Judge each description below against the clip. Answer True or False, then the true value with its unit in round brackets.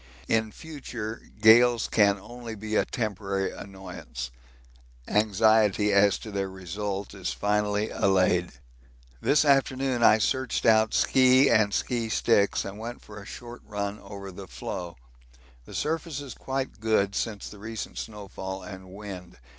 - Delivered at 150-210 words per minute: False (140 wpm)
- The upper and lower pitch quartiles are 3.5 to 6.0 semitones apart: False (2.8 semitones)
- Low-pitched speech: True (105 Hz)